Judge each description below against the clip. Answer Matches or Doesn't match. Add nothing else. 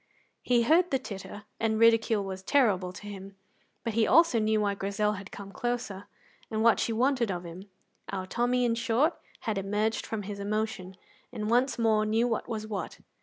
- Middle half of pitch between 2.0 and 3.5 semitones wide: Matches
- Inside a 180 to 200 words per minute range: Matches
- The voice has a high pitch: Matches